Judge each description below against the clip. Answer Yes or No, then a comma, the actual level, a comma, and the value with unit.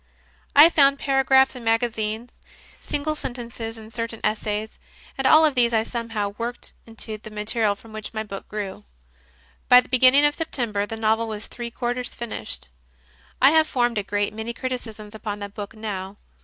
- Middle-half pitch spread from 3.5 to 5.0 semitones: No, average, 2.8 semitones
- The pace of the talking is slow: No, average, 170 wpm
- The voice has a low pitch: No, high, 225 Hz